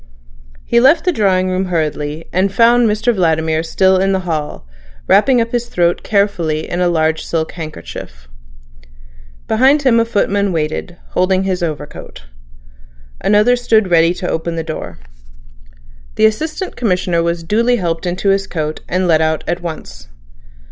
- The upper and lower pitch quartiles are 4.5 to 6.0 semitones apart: Yes, average, 4.9 semitones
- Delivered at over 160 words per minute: No, average, 155 wpm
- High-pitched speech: No, medium, 180 Hz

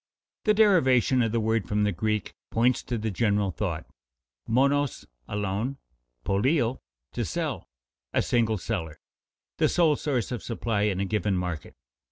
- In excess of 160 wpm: No, average, 155 wpm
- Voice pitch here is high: No, low, 110 Hz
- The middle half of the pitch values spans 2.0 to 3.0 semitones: No, average, 4.0 semitones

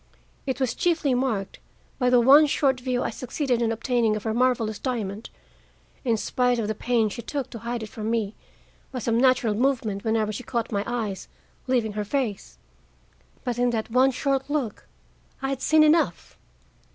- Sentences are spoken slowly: No, average, 180 wpm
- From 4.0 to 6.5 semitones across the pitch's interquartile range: No, average, 2.9 semitones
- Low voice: No, high, 240 Hz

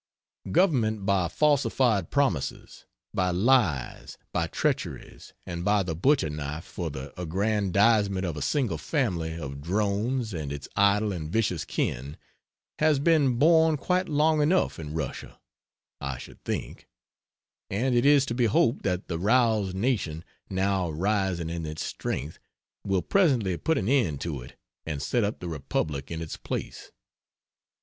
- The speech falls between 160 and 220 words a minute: No, average, 150 wpm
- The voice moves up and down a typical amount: No, wide, 7.3 semitones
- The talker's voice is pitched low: Yes, low, 100 Hz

